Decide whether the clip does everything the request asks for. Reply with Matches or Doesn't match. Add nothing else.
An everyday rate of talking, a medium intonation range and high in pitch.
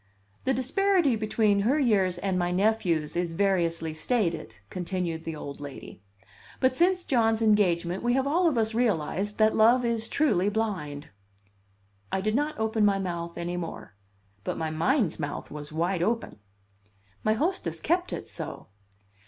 Doesn't match